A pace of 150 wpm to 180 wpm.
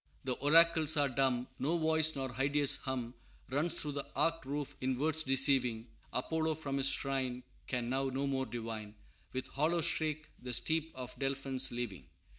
Yes: average, 165 wpm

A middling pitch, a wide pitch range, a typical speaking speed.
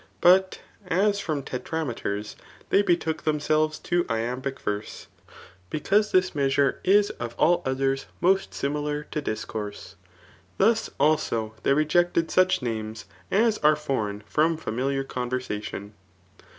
No: medium, 150 Hz; wide, 6.0 semitones; slow, 125 wpm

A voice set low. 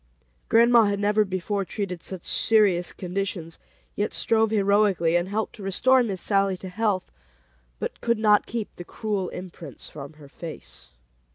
No: high, 195 Hz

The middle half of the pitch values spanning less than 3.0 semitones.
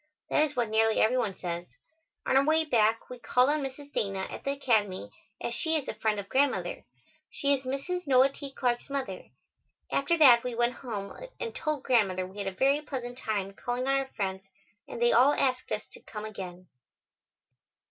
No: average, 4.7 semitones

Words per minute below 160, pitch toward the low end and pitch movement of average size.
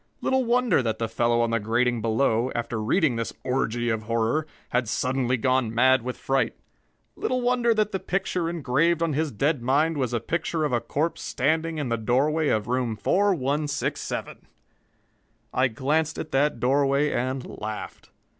No: average, 165 wpm; low, 130 Hz; average, 5.0 semitones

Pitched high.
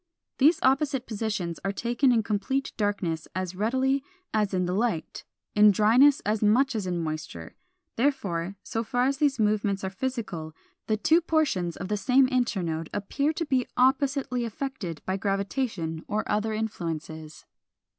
Yes: high, 215 Hz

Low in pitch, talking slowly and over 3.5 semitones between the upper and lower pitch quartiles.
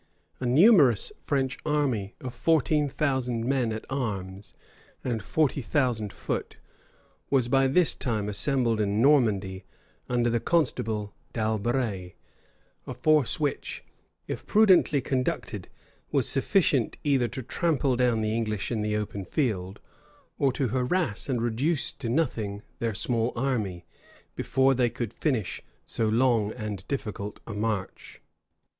Yes: low, 120 Hz; slow, 130 wpm; average, 4.1 semitones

